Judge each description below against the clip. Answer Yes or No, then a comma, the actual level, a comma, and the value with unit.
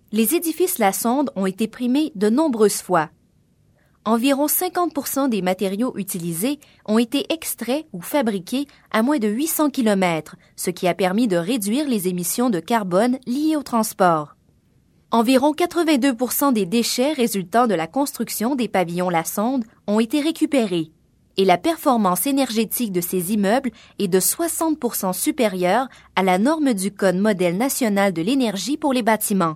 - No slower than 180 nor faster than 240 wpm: No, average, 155 wpm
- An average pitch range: No, wide, 6.1 semitones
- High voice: Yes, high, 230 Hz